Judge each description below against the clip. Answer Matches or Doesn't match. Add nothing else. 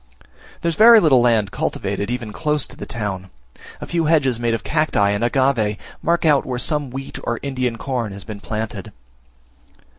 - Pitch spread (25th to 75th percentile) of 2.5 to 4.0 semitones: Doesn't match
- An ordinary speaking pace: Matches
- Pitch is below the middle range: Matches